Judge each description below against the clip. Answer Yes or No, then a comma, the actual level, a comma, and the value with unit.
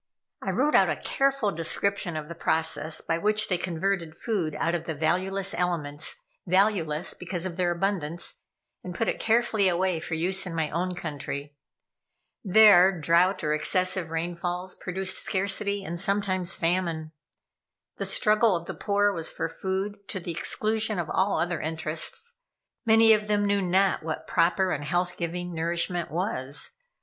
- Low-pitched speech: No, medium, 180 Hz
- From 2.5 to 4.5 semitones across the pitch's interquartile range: Yes, average, 3.2 semitones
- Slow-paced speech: No, average, 160 wpm